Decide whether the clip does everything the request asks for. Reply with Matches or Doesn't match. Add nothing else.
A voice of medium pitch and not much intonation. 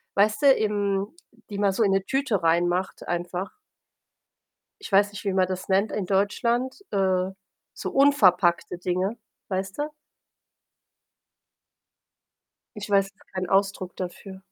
Doesn't match